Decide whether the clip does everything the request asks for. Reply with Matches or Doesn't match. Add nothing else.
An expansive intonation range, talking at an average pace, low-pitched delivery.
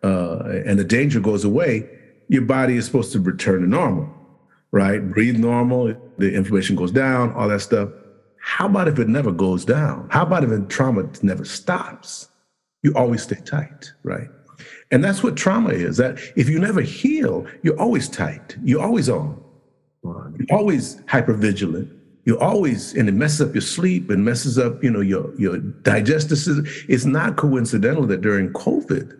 Matches